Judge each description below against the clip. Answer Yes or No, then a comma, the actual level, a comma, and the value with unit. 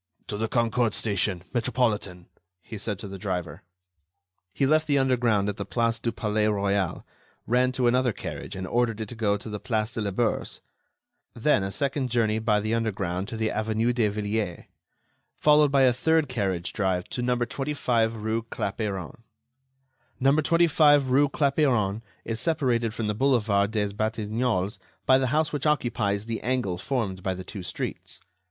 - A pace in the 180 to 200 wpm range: No, average, 170 wpm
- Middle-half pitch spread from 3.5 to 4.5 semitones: Yes, average, 3.8 semitones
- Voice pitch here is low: Yes, low, 115 Hz